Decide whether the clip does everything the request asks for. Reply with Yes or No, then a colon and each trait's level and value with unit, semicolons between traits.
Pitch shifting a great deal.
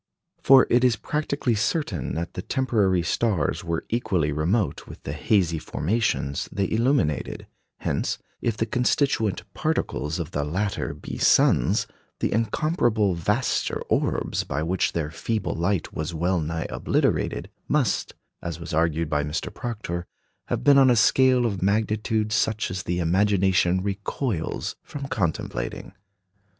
Yes: wide, 5.8 semitones